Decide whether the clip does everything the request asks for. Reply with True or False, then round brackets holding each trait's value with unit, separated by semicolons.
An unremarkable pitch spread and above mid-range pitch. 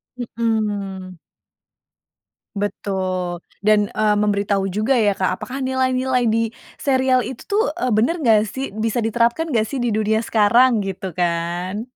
True (4.1 semitones; 215 Hz)